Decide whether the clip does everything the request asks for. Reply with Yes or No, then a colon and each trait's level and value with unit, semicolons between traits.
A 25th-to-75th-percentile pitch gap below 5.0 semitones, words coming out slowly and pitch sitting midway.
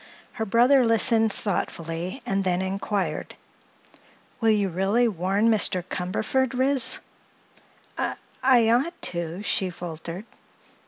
No: average, 4.5 semitones; slow, 105 wpm; high, 205 Hz